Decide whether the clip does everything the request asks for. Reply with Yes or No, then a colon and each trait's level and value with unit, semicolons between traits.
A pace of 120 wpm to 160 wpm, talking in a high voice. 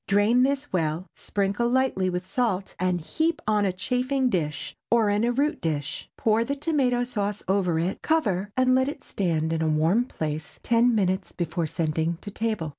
No: average, 185 wpm; high, 205 Hz